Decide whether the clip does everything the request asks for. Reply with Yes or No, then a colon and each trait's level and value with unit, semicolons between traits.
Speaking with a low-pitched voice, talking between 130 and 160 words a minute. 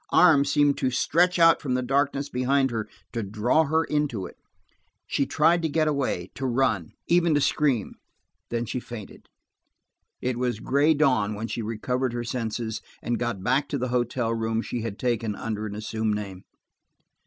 No: low, 125 Hz; average, 175 wpm